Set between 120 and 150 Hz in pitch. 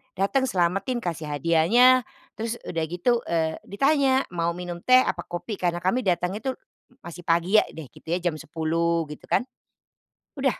No: medium, 175 Hz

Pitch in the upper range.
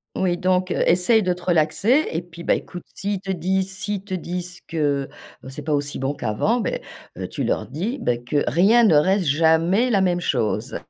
No: medium, 180 Hz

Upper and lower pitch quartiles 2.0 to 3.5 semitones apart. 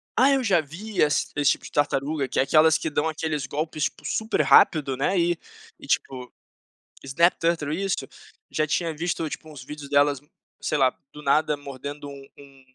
Yes: average, 2.7 semitones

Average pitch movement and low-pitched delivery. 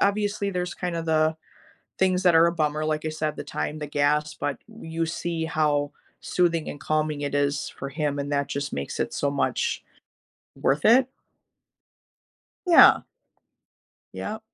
No: average, 3.0 semitones; medium, 155 Hz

